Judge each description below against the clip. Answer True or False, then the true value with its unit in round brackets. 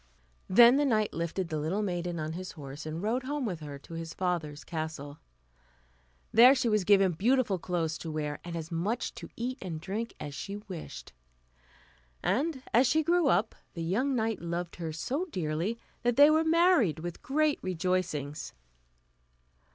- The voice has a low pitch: False (185 Hz)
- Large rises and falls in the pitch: True (6.9 semitones)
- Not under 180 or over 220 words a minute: False (170 wpm)